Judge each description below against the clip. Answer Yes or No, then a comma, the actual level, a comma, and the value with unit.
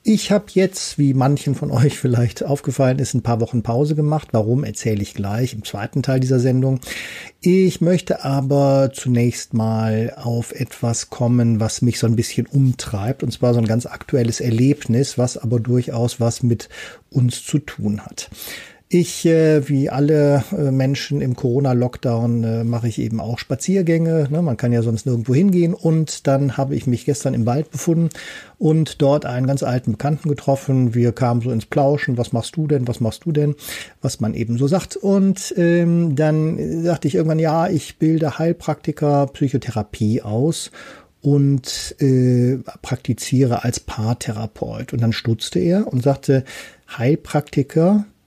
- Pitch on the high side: No, low, 135 Hz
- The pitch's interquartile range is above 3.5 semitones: Yes, average, 4.5 semitones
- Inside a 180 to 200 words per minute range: No, average, 160 wpm